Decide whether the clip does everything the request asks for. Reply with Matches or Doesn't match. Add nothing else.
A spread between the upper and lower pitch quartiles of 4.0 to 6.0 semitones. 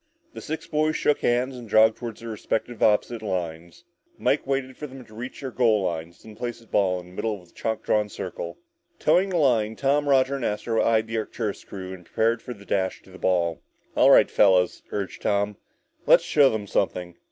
Matches